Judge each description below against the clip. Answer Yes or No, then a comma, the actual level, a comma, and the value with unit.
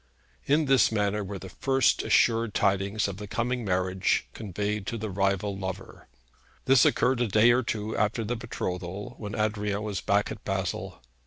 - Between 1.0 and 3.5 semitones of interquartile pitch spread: Yes, average, 2.7 semitones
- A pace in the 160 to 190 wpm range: Yes, average, 170 wpm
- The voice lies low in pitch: Yes, low, 105 Hz